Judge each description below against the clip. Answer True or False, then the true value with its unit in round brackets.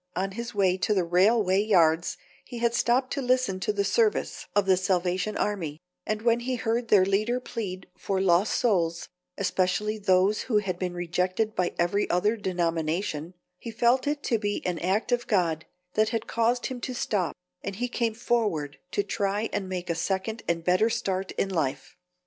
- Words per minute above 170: True (185 wpm)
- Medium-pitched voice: False (200 Hz)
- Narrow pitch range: False (3.9 semitones)